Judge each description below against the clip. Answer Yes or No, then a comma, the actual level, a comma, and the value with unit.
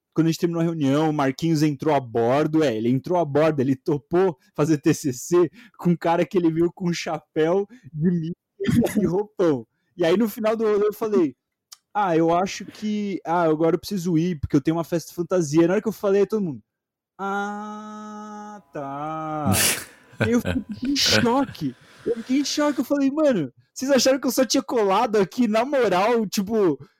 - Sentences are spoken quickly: Yes, fast, 200 wpm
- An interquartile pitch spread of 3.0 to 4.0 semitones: No, average, 5.2 semitones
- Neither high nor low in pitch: Yes, medium, 175 Hz